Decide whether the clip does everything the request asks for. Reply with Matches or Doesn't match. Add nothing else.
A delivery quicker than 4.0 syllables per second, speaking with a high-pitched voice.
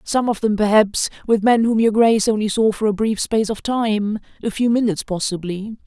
Matches